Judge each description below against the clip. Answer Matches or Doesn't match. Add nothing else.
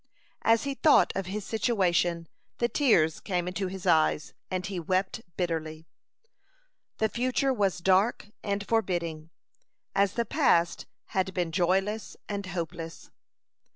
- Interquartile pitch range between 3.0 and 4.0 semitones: Matches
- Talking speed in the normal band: Doesn't match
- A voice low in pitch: Doesn't match